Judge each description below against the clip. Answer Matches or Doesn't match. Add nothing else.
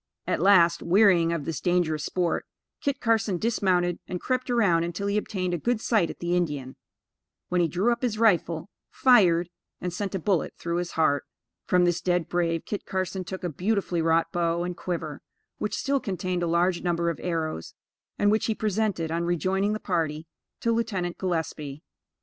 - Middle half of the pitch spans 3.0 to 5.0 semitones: Matches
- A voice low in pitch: Doesn't match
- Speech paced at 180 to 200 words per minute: Matches